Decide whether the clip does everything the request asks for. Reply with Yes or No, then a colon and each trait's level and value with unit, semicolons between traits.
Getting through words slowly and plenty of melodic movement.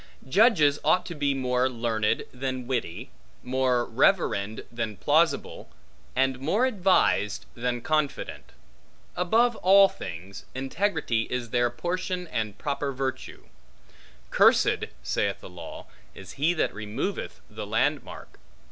Yes: slow, 120 wpm; wide, 6.7 semitones